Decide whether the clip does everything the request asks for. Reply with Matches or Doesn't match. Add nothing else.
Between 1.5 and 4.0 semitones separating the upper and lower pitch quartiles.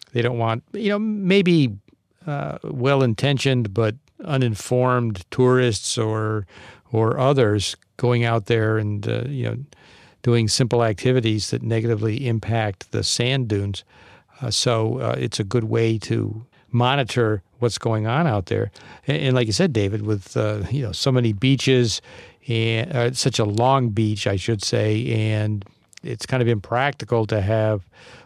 Matches